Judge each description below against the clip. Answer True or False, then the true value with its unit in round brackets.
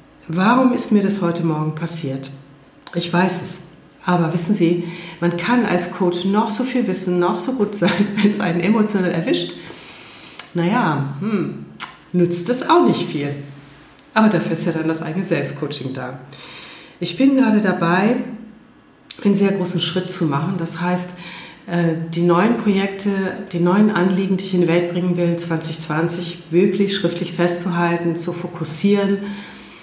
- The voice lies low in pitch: False (175 Hz)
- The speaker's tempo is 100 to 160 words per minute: True (155 wpm)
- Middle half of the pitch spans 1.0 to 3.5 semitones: True (2.9 semitones)